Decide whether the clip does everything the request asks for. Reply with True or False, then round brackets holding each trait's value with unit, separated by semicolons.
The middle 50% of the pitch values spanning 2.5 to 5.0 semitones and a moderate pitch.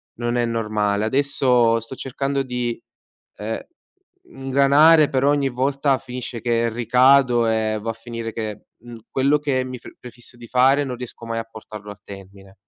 False (2.9 semitones; 120 Hz)